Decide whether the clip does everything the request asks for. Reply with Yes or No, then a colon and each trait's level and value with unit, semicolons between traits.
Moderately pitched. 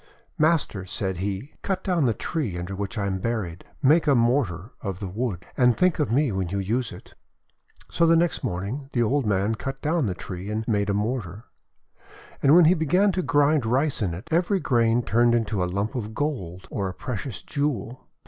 No: low, 115 Hz